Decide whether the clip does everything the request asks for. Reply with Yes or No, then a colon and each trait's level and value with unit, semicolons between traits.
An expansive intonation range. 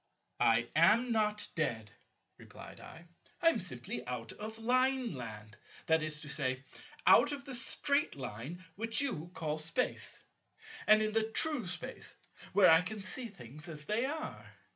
Yes: wide, 7.6 semitones